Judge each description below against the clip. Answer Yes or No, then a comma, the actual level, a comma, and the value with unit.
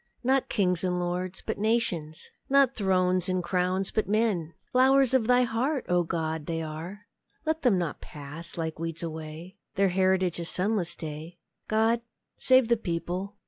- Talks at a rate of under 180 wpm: Yes, average, 160 wpm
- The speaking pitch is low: No, medium, 185 Hz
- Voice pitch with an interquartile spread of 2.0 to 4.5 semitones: No, average, 5.0 semitones